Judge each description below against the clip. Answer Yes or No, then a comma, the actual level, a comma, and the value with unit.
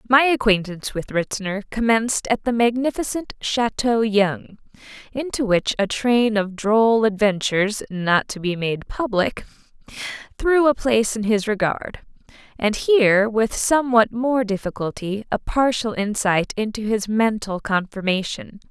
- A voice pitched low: No, high, 220 Hz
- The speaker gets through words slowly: Yes, slow, 130 wpm